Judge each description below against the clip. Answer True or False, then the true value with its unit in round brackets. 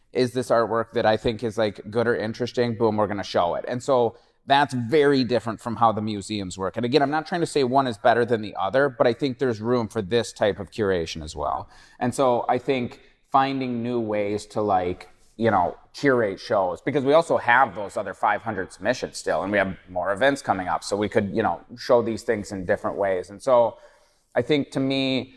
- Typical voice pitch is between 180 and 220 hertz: False (120 Hz)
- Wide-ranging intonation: False (4.1 semitones)